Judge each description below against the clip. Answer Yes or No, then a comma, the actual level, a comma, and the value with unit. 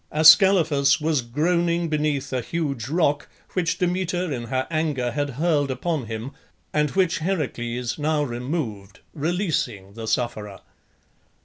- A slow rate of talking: Yes, slow, 125 wpm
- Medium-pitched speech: Yes, medium, 145 Hz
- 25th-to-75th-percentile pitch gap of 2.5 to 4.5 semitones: No, average, 5.2 semitones